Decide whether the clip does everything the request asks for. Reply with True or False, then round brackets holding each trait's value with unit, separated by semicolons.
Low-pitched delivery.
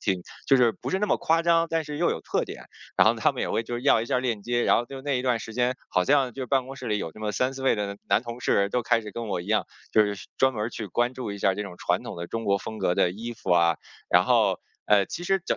True (120 Hz)